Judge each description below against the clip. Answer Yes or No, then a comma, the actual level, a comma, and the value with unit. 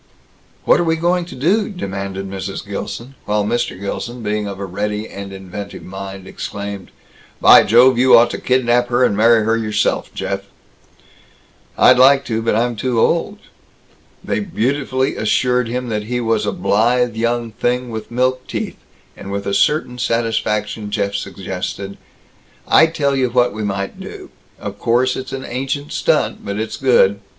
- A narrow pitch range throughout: No, average, 4.0 semitones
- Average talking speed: Yes, average, 165 wpm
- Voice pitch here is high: No, low, 115 Hz